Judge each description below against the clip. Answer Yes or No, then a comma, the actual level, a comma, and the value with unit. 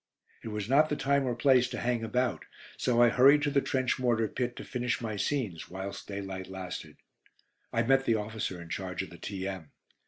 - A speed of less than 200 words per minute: No, fast, 205 wpm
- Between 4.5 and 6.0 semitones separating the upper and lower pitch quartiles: Yes, average, 4.8 semitones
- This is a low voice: Yes, low, 115 Hz